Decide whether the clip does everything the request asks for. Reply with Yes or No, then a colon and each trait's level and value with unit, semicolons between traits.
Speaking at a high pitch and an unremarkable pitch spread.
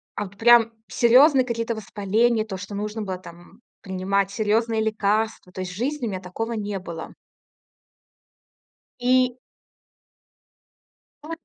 Yes: high, 215 Hz; average, 3.3 semitones